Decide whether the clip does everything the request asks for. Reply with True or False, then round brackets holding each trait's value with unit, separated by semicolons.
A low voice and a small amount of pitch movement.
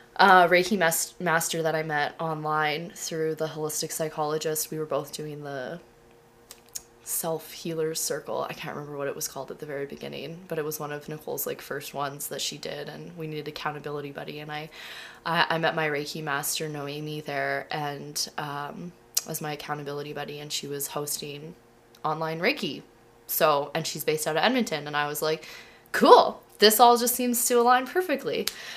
False (155 Hz; 2.0 semitones)